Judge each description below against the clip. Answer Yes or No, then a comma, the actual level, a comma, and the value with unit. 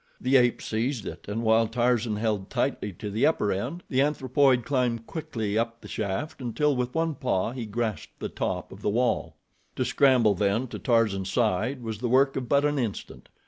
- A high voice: No, low, 120 Hz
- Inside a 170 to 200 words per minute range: Yes, average, 195 wpm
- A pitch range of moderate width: Yes, average, 3.4 semitones